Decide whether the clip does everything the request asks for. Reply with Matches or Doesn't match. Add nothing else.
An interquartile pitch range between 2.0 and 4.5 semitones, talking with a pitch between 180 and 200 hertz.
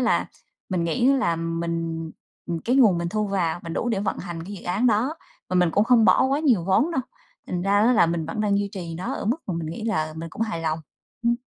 Doesn't match